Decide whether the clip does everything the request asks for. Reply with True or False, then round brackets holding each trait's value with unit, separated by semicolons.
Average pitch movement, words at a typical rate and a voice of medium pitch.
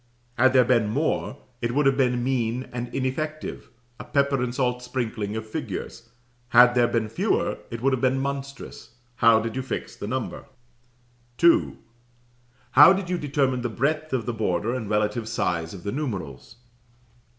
False (3.2 semitones; 170 wpm; 125 Hz)